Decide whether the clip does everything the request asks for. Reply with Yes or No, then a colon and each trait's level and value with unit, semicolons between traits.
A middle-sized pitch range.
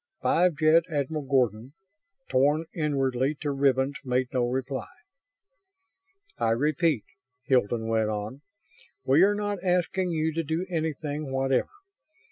Yes: average, 3.7 semitones